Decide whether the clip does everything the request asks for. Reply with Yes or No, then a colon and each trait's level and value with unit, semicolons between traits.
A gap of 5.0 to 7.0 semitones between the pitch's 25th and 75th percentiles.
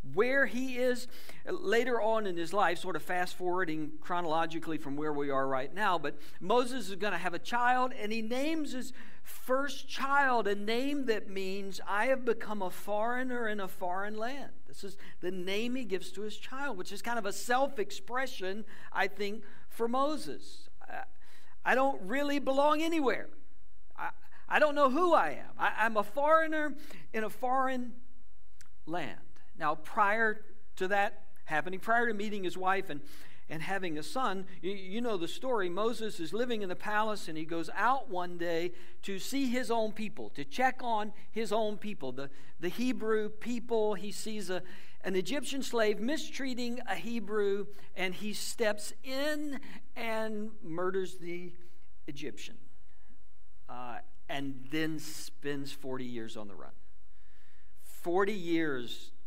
Yes: wide, 5.4 semitones